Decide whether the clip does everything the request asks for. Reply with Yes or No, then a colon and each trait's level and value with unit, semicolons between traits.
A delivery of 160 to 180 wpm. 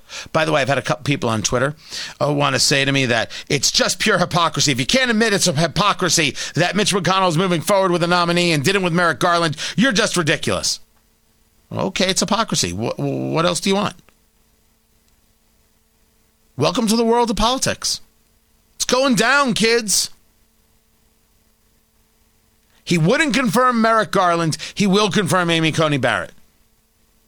Yes: average, 165 wpm